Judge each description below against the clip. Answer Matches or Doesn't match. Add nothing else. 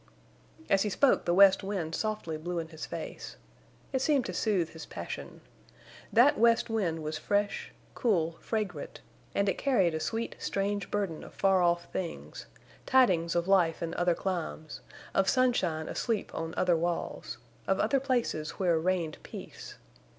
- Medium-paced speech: Matches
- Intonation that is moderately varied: Matches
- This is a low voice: Doesn't match